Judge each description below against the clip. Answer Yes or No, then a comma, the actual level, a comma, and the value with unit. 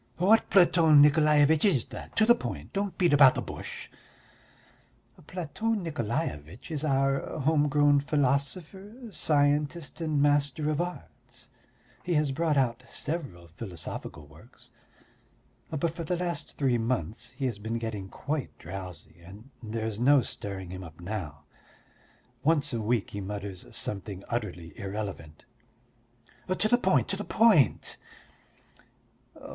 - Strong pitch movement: Yes, wide, 7.4 semitones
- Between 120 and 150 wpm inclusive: Yes, slow, 135 wpm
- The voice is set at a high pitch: No, medium, 140 Hz